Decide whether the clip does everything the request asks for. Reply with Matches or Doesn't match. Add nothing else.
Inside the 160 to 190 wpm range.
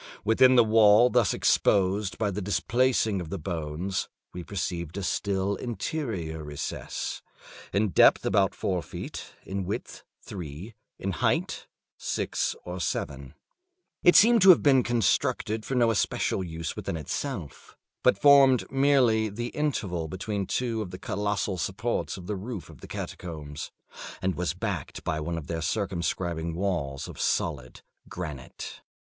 Doesn't match